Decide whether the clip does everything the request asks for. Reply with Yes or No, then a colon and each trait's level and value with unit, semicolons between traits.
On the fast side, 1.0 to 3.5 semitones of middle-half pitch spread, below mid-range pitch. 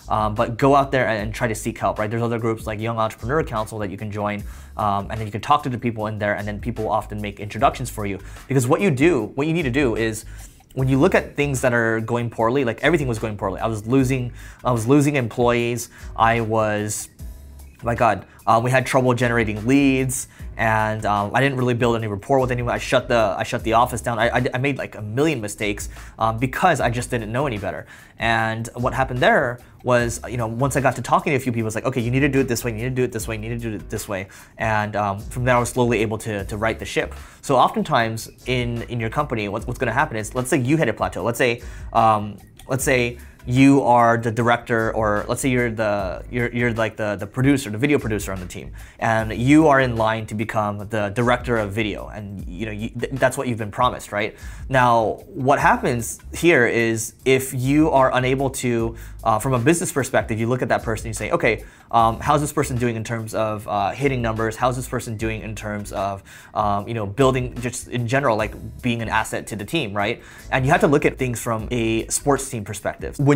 Yes: fast, 250 wpm; average, 3.0 semitones; low, 115 Hz